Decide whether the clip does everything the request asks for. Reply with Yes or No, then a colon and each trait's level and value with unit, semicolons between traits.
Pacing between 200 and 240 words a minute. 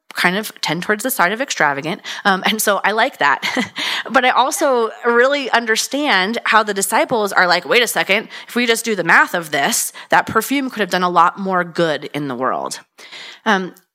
Yes: fast, 205 wpm